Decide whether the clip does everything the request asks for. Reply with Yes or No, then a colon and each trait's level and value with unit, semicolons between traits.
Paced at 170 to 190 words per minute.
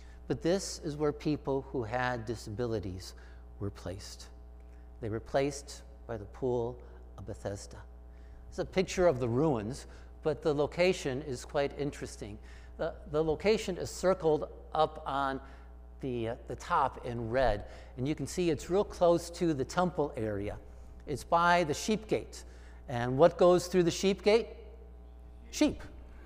No: average, 155 wpm